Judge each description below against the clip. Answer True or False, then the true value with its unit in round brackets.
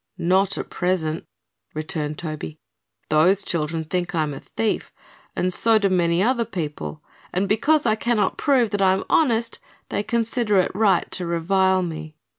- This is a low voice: False (185 Hz)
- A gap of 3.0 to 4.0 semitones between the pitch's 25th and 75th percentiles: False (5.0 semitones)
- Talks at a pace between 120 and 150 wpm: False (165 wpm)